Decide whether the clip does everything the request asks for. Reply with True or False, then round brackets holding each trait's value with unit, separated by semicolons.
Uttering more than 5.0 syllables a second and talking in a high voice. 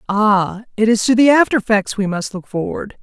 True (5.2 syllables/s; 215 Hz)